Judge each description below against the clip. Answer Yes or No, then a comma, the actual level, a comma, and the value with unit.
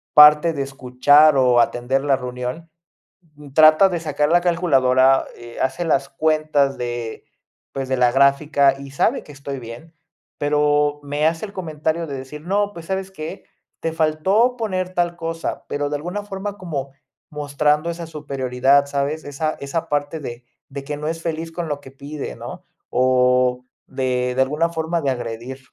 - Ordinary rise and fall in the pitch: Yes, average, 3.5 semitones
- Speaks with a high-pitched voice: No, medium, 145 Hz